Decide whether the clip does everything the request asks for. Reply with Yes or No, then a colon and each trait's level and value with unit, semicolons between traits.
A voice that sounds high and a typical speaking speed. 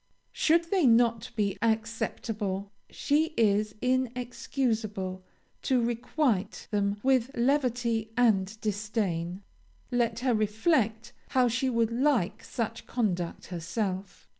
No: high, 225 Hz; slow, 105 wpm